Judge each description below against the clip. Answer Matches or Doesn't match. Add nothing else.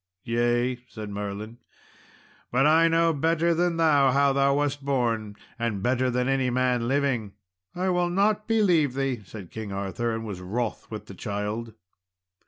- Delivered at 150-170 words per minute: Matches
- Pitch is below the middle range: Matches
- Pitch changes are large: Doesn't match